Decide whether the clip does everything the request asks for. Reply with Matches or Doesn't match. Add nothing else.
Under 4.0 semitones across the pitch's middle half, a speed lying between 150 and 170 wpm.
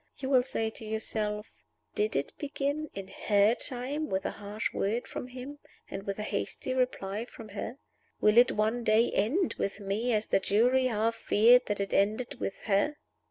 Doesn't match